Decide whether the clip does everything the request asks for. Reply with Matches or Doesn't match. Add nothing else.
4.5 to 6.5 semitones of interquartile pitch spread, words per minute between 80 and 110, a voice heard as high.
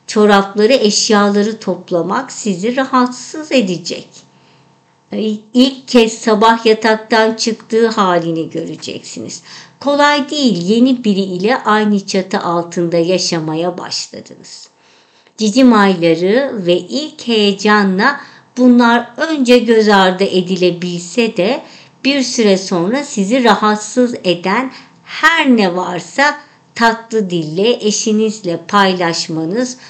Matches